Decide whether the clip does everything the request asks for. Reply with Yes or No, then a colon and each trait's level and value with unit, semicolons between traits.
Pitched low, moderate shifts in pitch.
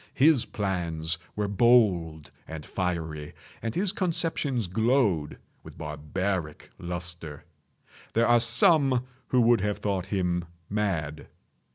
No: very low, 95 Hz; wide, 6.4 semitones